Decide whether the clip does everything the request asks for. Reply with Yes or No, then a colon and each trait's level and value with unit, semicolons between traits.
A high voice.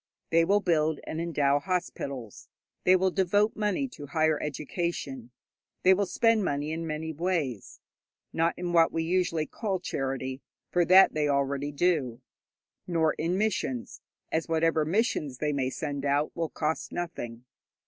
No: medium, 160 Hz